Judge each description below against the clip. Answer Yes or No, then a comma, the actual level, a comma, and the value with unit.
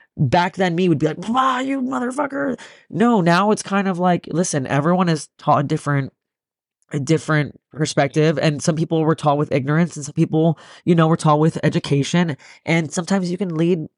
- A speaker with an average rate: Yes, average, 195 wpm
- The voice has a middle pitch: Yes, medium, 165 Hz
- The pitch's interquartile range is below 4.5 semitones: Yes, average, 3.3 semitones